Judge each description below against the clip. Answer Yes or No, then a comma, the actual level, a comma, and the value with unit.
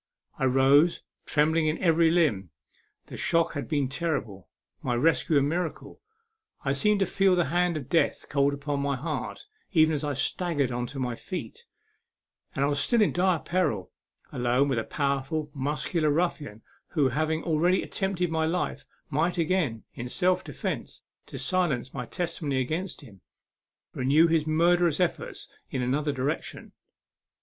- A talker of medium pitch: Yes, medium, 150 Hz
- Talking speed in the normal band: Yes, average, 155 wpm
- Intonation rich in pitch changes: No, average, 3.9 semitones